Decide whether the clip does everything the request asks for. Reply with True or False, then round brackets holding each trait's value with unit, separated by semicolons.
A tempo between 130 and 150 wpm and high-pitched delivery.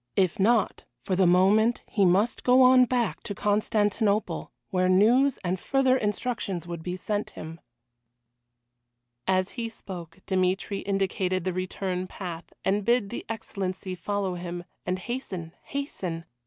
True (140 wpm; 195 Hz)